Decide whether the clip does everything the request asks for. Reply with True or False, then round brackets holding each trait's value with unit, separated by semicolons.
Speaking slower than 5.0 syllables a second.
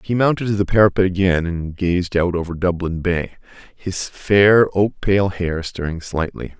True (4.6 syllables/s)